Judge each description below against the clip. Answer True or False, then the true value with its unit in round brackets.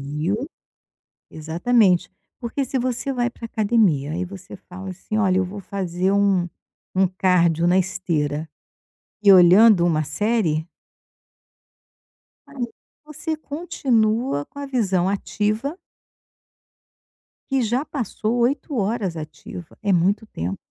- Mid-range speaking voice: False (200 Hz)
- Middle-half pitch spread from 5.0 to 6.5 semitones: True (5.3 semitones)